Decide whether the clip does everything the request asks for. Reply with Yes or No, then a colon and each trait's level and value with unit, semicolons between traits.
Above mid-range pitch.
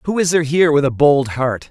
No: medium, 145 Hz